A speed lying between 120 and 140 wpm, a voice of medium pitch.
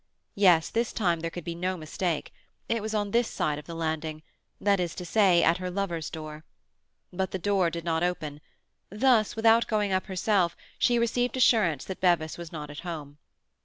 No: average, 190 wpm; medium, 180 Hz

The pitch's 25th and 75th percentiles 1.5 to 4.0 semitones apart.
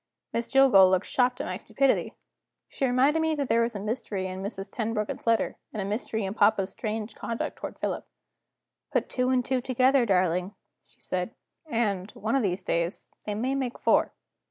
No: average, 4.5 semitones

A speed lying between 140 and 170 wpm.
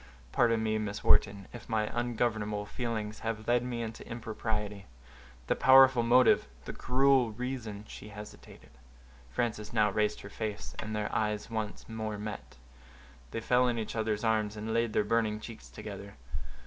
Yes: average, 150 wpm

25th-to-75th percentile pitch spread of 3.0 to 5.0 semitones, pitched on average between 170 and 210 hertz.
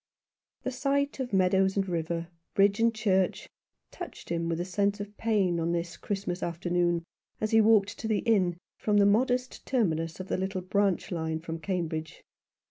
Yes: average, 3.8 semitones; high, 190 Hz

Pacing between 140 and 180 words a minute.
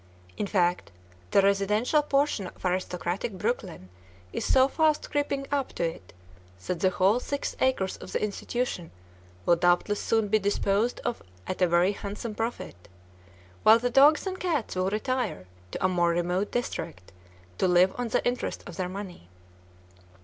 Yes: average, 160 wpm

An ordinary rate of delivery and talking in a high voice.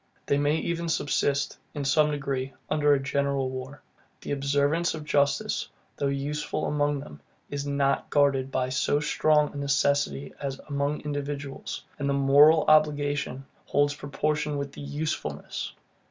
No: average, 145 wpm; medium, 145 Hz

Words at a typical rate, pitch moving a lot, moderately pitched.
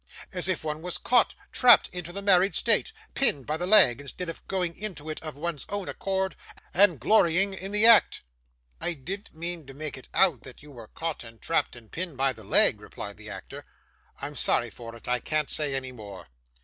No: fast, 210 wpm; wide, 5.9 semitones; medium, 165 Hz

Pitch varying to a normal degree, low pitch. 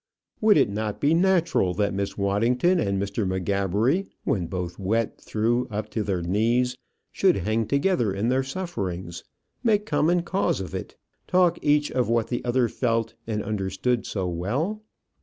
No: wide, 6.2 semitones; low, 115 Hz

